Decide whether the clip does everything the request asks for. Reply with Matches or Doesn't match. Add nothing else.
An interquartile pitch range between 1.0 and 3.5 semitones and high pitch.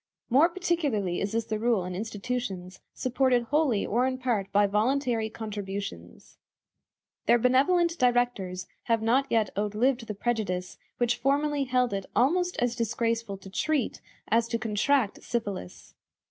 Doesn't match